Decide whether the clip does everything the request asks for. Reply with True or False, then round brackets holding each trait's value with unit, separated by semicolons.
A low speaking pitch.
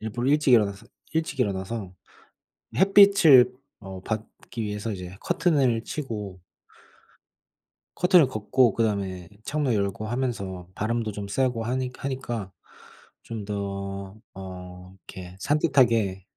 True (110 Hz)